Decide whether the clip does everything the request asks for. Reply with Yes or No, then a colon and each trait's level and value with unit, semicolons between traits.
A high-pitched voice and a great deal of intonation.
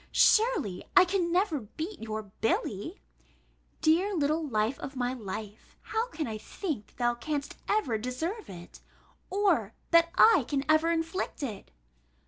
Yes: very high, 295 Hz; wide, 8.0 semitones